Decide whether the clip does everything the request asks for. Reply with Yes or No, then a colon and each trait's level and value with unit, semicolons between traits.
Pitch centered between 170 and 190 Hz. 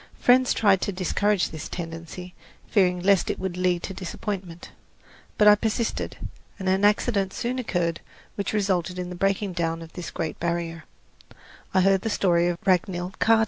Yes: medium, 185 Hz